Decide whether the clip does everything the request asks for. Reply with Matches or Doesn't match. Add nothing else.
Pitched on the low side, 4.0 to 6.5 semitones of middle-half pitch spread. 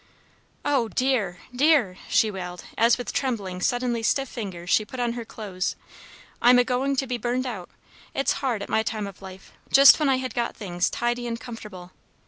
Doesn't match